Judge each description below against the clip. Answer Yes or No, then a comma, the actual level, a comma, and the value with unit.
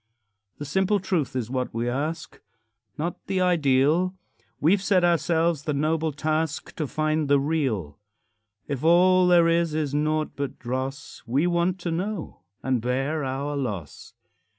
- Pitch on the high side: No, medium, 155 Hz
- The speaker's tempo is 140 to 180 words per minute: Yes, average, 150 wpm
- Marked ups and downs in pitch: No, average, 4.0 semitones